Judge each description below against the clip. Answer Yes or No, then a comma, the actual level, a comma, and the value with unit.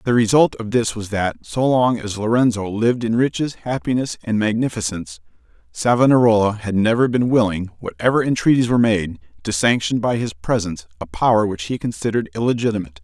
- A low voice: Yes, low, 110 Hz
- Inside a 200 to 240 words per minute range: No, average, 165 wpm